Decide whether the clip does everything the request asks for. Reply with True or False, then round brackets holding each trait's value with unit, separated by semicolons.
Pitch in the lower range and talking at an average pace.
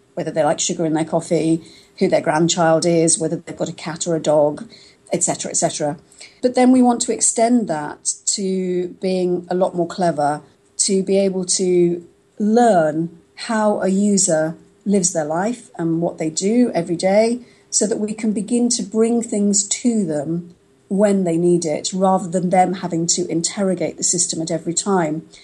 False (180 Hz; 185 wpm)